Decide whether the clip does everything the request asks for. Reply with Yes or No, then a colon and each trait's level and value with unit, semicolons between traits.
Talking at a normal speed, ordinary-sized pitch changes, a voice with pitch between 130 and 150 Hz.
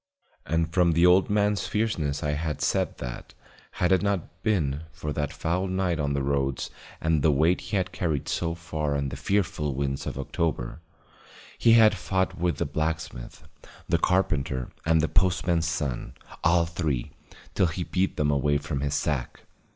No: average, 175 wpm; average, 4.0 semitones; very low, 80 Hz